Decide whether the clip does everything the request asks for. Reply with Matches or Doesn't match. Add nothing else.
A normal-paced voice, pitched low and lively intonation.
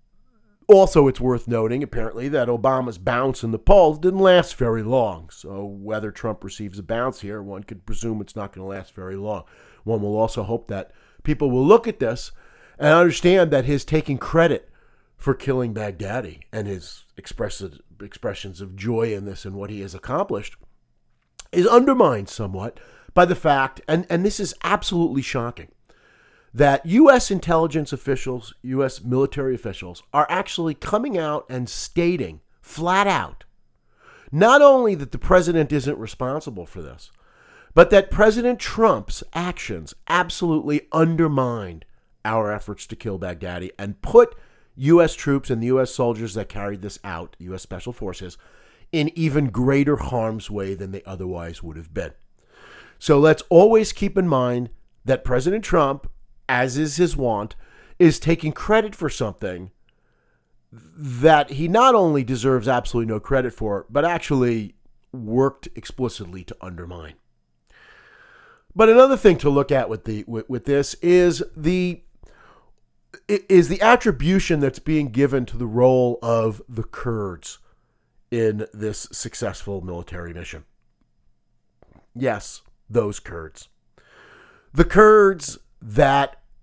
Matches